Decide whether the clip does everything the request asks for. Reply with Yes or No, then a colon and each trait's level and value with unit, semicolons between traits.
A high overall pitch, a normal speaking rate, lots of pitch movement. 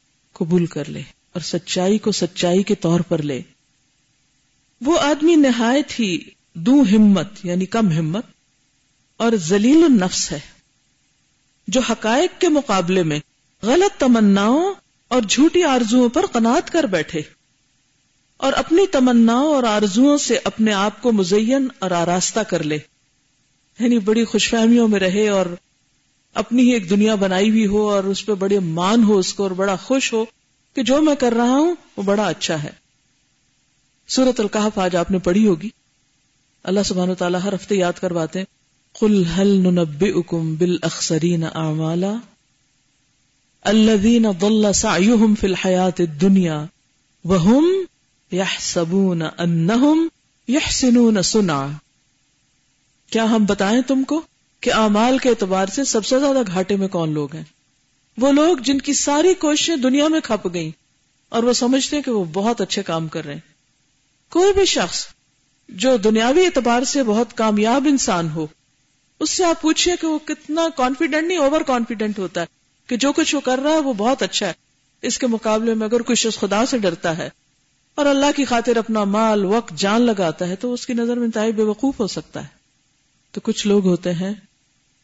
Yes: high, 200 Hz; average, 165 wpm; wide, 7.2 semitones